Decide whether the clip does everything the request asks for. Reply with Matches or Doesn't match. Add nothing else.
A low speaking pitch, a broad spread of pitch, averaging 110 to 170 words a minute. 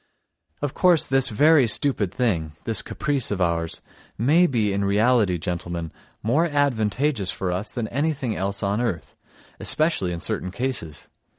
Matches